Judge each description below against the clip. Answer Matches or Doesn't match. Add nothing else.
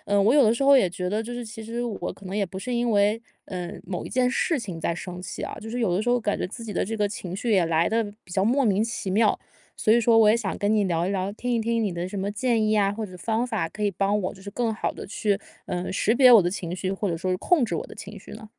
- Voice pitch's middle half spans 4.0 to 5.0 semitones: Doesn't match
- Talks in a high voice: Matches